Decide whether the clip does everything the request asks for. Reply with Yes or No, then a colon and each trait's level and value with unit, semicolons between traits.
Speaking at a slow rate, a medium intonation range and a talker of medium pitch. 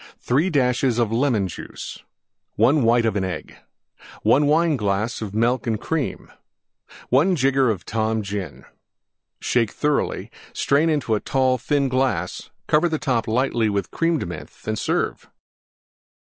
No: slow, 130 wpm; average, 4.5 semitones; low, 125 Hz